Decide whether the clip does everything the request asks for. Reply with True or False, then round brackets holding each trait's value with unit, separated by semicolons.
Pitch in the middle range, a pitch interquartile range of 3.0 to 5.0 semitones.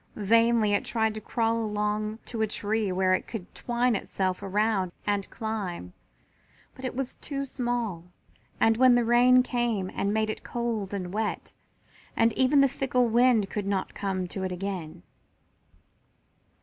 False (220 Hz; 3.4 semitones)